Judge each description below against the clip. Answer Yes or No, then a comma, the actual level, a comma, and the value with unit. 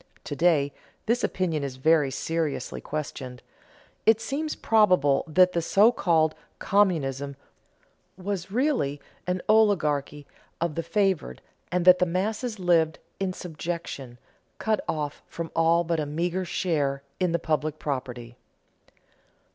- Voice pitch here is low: No, medium, 165 Hz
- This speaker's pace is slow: Yes, slow, 130 wpm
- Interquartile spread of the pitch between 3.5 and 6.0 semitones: Yes, average, 4.2 semitones